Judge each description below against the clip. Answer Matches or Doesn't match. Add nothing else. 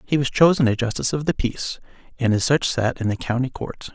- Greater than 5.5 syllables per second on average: Matches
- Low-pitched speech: Matches